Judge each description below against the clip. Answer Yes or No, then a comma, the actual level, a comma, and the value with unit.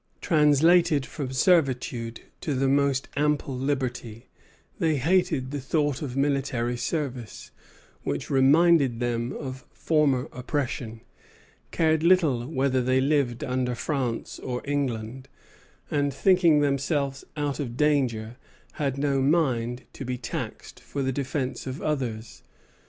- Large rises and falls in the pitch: No, average, 2.8 semitones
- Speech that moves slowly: Yes, slow, 125 wpm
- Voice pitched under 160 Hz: Yes, low, 135 Hz